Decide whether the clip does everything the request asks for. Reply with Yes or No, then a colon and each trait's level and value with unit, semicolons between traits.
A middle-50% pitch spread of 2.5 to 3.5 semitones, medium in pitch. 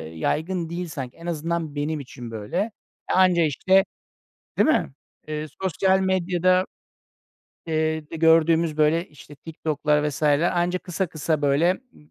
Yes: average, 3.0 semitones; medium, 160 Hz